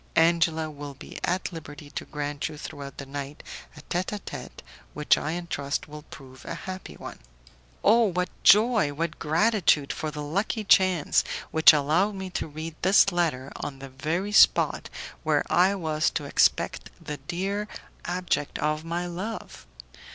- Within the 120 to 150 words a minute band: No, average, 160 wpm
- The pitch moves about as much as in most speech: Yes, average, 4.1 semitones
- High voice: No, medium, 160 Hz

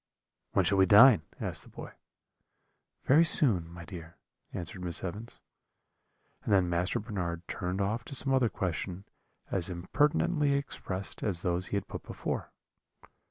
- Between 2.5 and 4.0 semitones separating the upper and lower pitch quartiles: No, average, 5.0 semitones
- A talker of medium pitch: No, very low, 95 Hz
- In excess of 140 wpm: Yes, average, 150 wpm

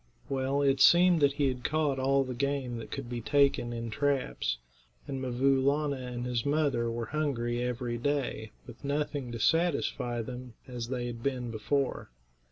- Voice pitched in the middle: No, low, 130 Hz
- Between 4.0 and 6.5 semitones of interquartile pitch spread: No, average, 2.8 semitones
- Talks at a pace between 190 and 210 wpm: No, average, 175 wpm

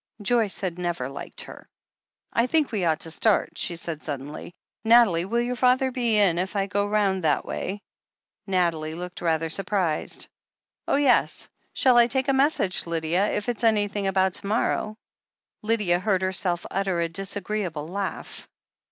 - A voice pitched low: No, high, 195 Hz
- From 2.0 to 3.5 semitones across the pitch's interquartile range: No, average, 4.3 semitones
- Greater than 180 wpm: No, average, 170 wpm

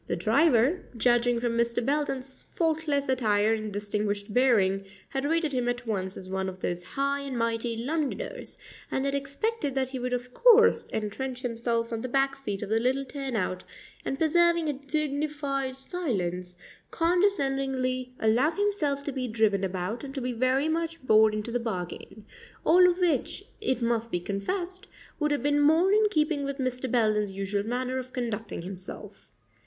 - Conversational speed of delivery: Yes, average, 170 wpm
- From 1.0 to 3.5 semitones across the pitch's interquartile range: No, average, 4.8 semitones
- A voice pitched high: Yes, very high, 255 Hz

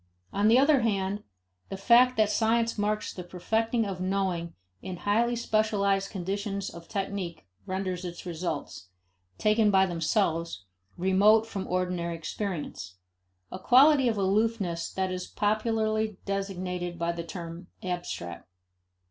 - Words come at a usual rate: No, slow, 130 wpm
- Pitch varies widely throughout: No, average, 3.4 semitones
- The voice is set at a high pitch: Yes, high, 195 Hz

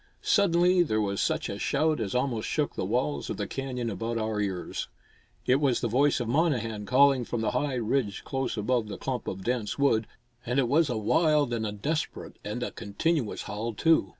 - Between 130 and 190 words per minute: No, fast, 205 wpm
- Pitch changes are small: No, average, 4.5 semitones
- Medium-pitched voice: No, low, 125 Hz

